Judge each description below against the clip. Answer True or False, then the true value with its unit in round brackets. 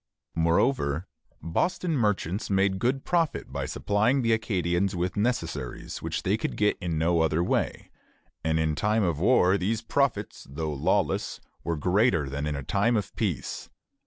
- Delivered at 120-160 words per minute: True (155 wpm)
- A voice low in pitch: True (95 Hz)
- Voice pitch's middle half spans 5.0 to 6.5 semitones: True (5.4 semitones)